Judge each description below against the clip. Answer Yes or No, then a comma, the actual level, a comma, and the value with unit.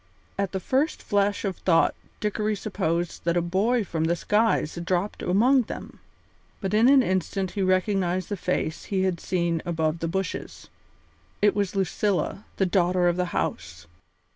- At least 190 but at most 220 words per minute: No, average, 165 wpm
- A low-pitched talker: No, medium, 185 Hz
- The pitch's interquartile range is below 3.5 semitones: Yes, average, 2.9 semitones